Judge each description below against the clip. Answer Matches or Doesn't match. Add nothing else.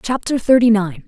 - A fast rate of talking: Doesn't match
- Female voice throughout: Matches